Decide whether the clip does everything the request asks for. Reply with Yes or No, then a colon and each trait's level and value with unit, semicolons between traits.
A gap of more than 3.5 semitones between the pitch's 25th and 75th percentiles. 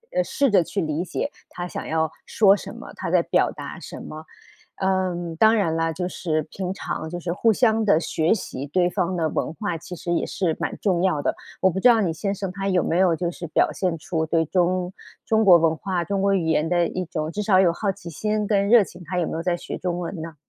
No: average, 3.1 semitones